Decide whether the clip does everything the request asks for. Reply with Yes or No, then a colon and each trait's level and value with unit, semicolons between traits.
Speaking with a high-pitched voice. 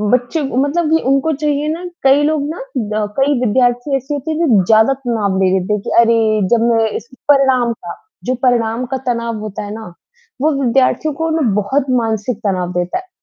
Yes: high, 245 Hz